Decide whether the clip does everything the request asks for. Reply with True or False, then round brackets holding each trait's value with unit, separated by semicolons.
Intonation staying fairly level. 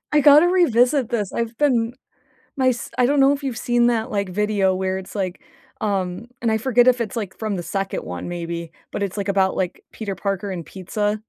False (4.2 semitones)